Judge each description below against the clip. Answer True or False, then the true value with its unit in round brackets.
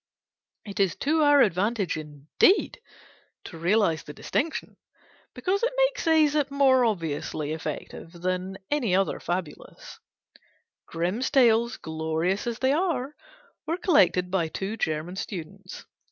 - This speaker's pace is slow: True (125 wpm)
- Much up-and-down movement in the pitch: True (8.6 semitones)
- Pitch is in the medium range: False (195 Hz)